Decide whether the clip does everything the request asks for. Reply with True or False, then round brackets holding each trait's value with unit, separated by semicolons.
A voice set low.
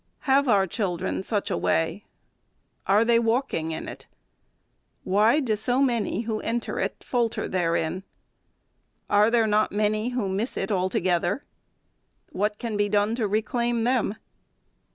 False (215 Hz)